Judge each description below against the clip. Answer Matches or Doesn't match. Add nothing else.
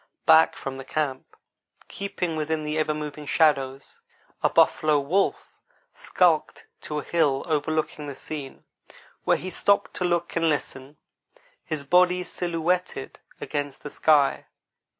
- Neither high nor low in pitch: Matches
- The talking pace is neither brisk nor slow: Doesn't match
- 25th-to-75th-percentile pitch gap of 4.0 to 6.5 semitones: Doesn't match